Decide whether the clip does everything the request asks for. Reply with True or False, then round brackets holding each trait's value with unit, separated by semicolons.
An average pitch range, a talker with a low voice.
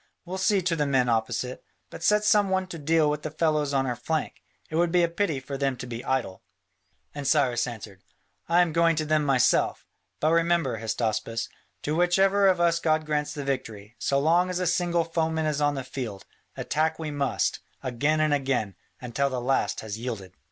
False (4.7 semitones; 150 Hz)